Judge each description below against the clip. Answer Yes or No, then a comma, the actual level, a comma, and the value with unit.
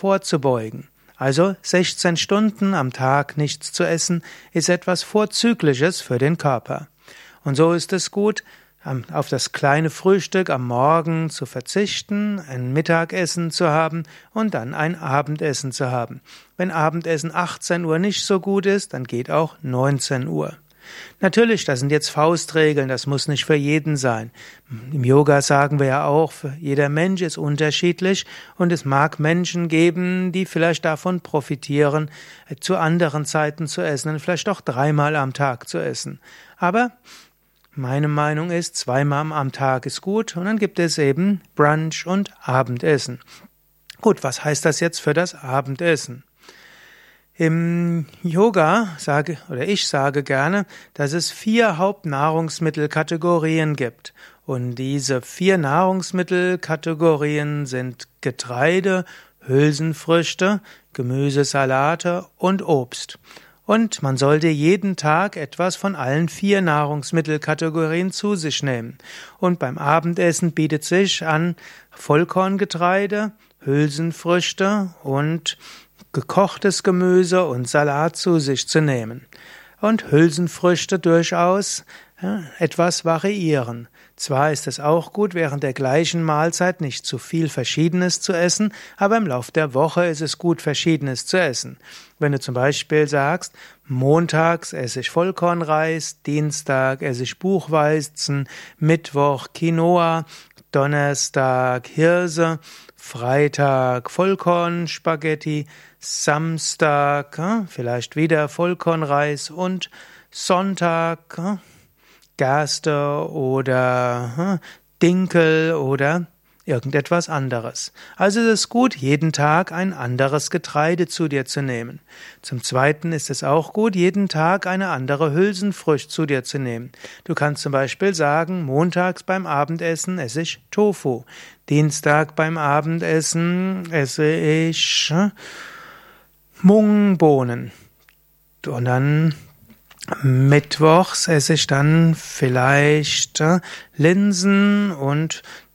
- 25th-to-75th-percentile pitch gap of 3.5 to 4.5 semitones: Yes, average, 3.8 semitones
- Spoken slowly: Yes, slow, 120 wpm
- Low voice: No, medium, 160 Hz